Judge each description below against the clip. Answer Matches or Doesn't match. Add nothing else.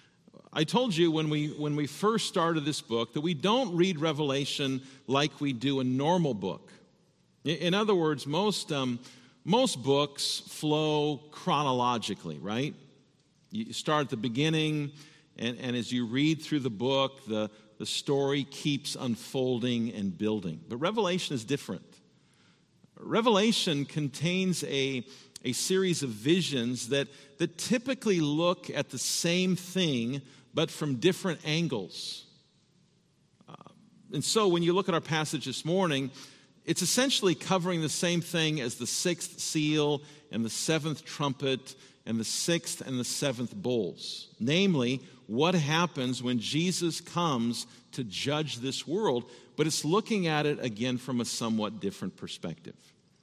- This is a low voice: Doesn't match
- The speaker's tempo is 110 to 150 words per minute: Matches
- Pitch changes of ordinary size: Matches